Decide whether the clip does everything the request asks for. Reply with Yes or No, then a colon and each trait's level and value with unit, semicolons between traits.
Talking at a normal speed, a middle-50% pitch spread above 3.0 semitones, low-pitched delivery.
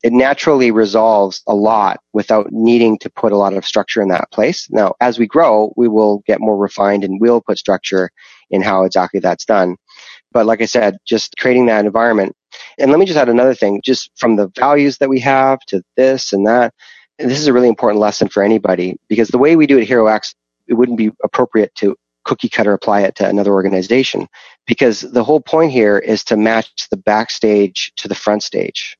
No: fast, 210 wpm; average, 3.4 semitones; low, 110 Hz